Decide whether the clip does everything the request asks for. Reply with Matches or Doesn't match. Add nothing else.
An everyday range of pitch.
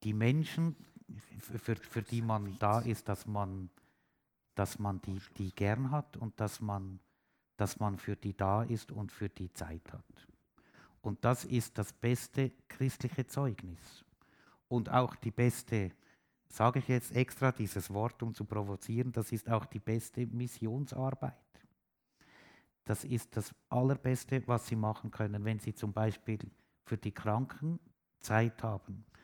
Matches